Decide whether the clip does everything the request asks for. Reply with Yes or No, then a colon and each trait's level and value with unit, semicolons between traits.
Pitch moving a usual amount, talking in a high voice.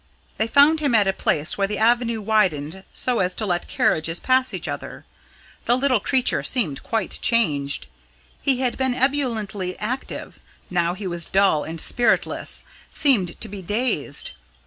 No: wide, 5.7 semitones; high, 215 Hz